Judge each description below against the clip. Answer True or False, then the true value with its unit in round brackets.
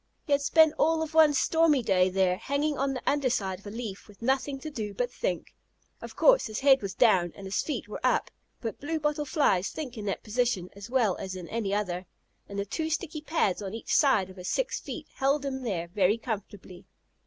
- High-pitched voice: True (235 Hz)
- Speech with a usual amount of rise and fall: False (6.8 semitones)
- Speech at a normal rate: False (225 wpm)